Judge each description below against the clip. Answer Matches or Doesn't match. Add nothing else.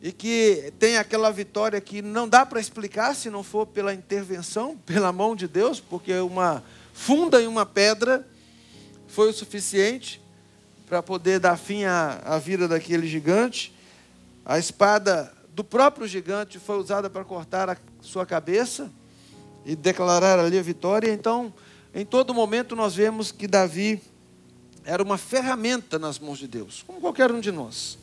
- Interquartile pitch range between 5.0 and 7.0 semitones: Doesn't match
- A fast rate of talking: Doesn't match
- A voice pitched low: Doesn't match